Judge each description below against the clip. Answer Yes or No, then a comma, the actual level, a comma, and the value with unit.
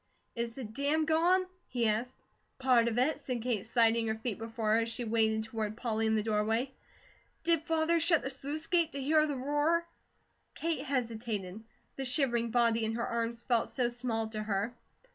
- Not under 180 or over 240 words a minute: Yes, average, 185 wpm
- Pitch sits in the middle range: No, high, 235 Hz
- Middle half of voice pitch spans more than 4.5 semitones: No, average, 4.1 semitones